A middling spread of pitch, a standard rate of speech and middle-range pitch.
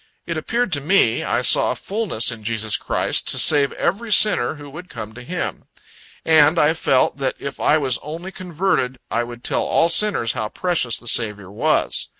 No: wide, 6.8 semitones; average, 190 wpm; medium, 145 Hz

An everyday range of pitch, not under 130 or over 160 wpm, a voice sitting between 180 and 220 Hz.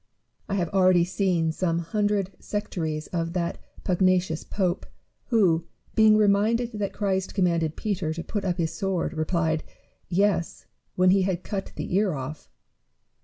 Yes: average, 3.0 semitones; average, 145 wpm; medium, 185 Hz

